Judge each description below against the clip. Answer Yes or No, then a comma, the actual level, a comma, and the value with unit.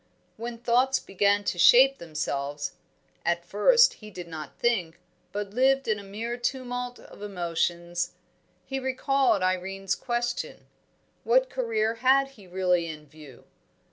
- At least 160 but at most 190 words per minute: No, slow, 135 wpm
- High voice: Yes, high, 210 Hz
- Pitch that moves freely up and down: Yes, wide, 6.1 semitones